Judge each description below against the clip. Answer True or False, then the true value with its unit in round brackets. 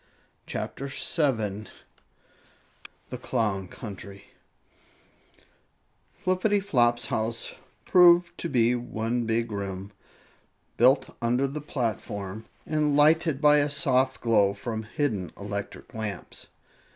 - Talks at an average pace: False (95 wpm)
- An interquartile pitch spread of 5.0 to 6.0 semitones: True (5.6 semitones)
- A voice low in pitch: True (120 Hz)